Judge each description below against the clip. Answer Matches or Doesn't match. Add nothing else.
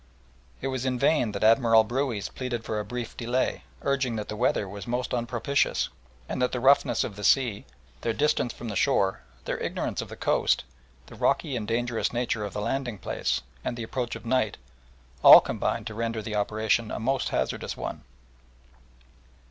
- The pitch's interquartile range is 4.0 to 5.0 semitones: Doesn't match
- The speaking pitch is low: Matches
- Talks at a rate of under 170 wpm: Doesn't match